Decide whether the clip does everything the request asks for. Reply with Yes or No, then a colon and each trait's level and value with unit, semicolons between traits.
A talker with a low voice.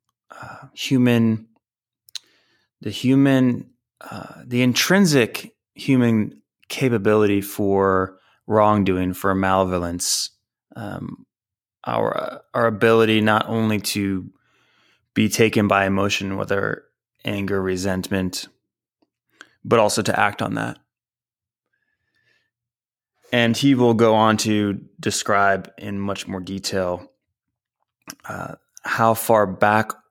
Yes: low, 105 Hz